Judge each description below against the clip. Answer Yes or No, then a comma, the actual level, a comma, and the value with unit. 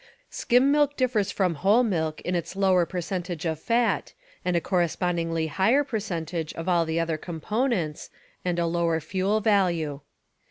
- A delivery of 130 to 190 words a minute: Yes, average, 155 wpm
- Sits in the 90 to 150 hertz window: No, medium, 180 Hz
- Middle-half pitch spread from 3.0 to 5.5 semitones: Yes, average, 4.1 semitones